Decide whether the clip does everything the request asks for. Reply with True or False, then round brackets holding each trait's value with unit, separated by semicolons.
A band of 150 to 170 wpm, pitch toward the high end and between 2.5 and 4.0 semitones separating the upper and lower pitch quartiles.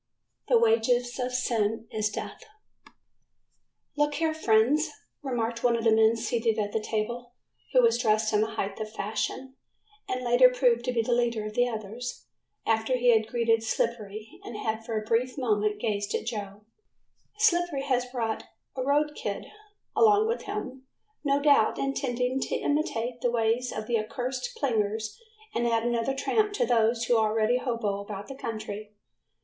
True (165 wpm; 235 Hz; 2.9 semitones)